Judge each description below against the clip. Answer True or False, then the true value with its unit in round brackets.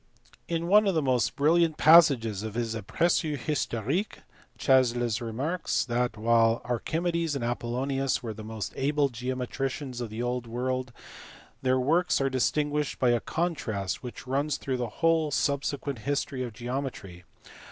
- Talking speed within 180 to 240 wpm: False (150 wpm)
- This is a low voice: True (130 Hz)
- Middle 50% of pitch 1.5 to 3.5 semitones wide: False (4.0 semitones)